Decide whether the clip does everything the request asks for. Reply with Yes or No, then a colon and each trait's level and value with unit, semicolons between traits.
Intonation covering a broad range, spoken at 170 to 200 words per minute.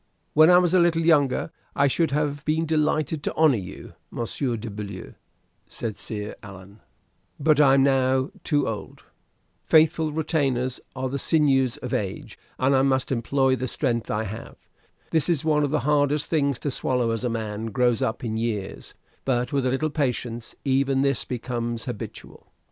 No: average, 4.1 semitones; average, 175 wpm